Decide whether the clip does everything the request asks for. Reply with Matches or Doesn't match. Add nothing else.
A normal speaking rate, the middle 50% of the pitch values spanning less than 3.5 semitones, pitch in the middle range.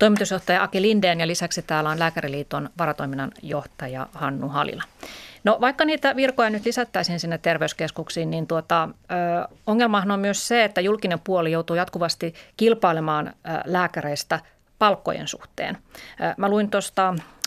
Doesn't match